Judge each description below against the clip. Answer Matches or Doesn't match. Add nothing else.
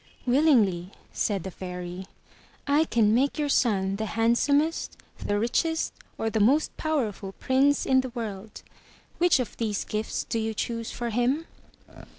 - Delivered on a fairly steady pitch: Doesn't match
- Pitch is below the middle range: Doesn't match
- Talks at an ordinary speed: Matches